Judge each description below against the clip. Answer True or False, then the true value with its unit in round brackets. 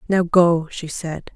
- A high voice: False (170 Hz)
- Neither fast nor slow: True (175 wpm)